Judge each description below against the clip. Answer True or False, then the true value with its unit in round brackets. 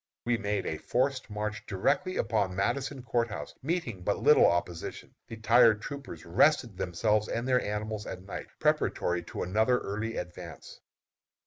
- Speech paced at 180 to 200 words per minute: False (150 wpm)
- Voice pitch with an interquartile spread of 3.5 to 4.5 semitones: True (4.1 semitones)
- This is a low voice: True (110 Hz)